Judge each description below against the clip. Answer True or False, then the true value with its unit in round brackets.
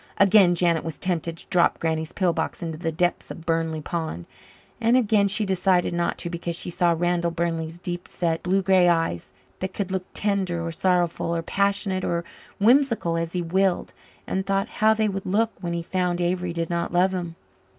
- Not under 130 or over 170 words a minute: False (195 wpm)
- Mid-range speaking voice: True (175 Hz)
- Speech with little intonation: True (2.3 semitones)